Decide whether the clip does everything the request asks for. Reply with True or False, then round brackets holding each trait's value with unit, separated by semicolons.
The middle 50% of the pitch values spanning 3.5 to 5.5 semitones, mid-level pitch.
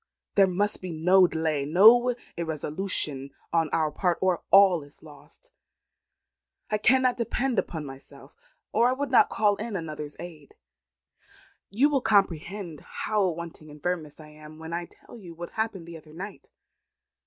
True (5.0 semitones; 175 Hz)